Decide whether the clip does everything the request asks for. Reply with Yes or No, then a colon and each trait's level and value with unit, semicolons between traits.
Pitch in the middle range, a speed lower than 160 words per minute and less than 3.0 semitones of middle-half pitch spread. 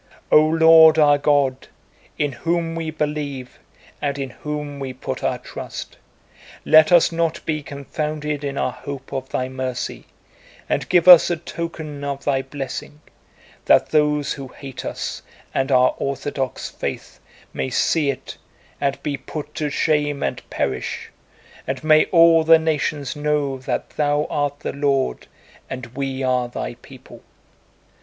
Yes: medium, 145 Hz; average, 150 wpm; narrow, 2.4 semitones